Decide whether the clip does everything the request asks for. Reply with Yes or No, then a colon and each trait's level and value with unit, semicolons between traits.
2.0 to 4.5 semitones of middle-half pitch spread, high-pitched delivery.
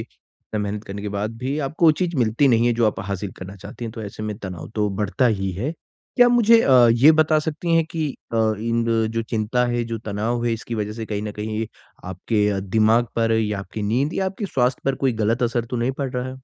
No: average, 3.8 semitones; low, 115 Hz